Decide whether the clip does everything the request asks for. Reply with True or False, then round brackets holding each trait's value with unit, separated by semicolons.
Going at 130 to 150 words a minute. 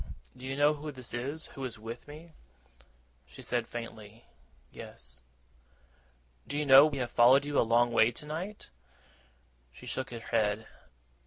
False (160 wpm)